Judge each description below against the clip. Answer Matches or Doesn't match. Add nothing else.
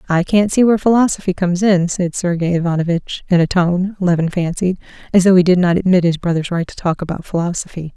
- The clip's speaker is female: Matches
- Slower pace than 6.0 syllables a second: Doesn't match